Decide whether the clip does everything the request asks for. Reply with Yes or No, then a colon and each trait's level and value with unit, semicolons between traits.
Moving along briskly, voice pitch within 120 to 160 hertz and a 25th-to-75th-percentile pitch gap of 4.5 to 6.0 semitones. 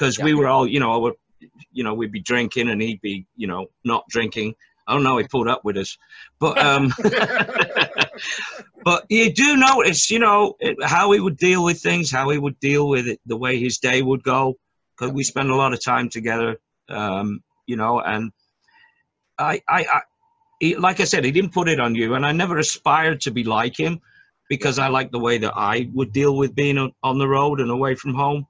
Yes: fast, 220 wpm; low, 135 Hz; wide, 5.5 semitones